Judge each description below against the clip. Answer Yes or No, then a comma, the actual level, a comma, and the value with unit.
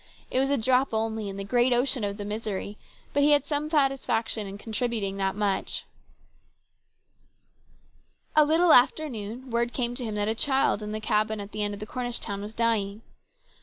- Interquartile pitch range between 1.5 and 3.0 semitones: No, average, 3.7 semitones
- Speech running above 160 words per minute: Yes, average, 190 wpm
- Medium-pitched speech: No, high, 225 Hz